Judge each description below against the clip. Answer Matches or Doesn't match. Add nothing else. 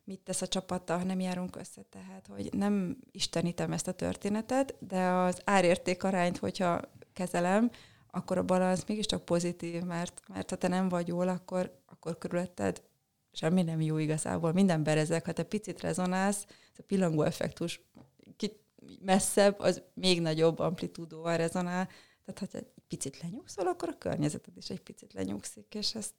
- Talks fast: Matches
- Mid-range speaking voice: Matches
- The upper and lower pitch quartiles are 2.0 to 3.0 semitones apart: Matches